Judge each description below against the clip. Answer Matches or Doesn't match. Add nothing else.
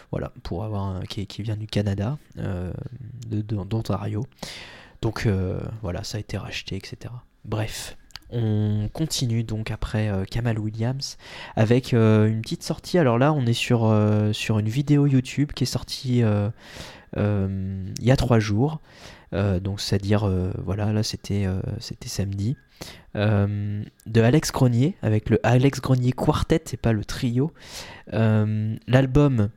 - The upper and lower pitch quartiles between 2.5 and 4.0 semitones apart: Matches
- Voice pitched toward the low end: Matches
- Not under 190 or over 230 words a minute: Doesn't match